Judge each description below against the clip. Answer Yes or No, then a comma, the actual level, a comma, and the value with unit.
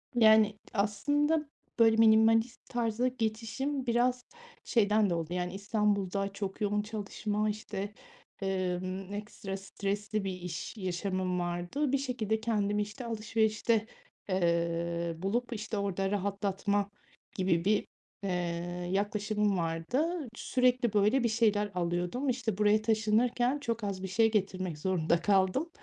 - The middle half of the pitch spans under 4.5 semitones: Yes, average, 3.0 semitones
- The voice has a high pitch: Yes, high, 210 Hz